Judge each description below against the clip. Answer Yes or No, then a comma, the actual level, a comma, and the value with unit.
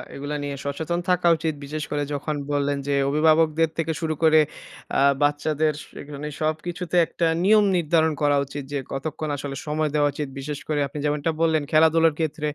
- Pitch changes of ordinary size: No, narrow, 1.8 semitones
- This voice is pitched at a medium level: Yes, medium, 155 Hz